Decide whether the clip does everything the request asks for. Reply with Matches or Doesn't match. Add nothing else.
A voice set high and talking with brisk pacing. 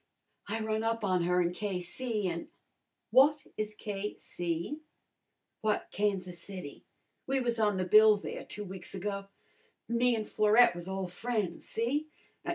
Doesn't match